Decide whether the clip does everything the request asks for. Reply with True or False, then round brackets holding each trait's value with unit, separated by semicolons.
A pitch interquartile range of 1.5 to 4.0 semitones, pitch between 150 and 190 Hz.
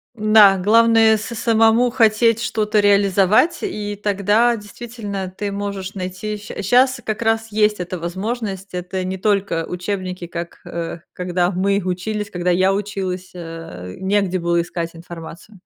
False (3.0 semitones; 200 Hz)